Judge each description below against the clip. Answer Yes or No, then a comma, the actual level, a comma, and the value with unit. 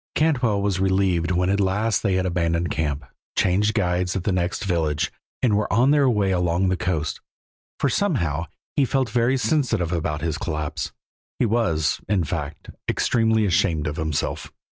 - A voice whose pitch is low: Yes, very low, 95 Hz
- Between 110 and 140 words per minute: No, average, 165 wpm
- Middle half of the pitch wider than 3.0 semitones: Yes, average, 4.5 semitones